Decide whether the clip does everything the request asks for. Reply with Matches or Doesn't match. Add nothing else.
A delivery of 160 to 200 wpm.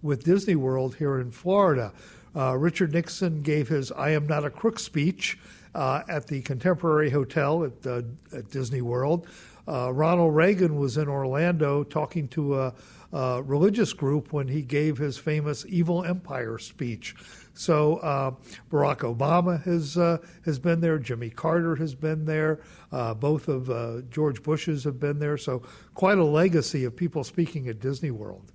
Matches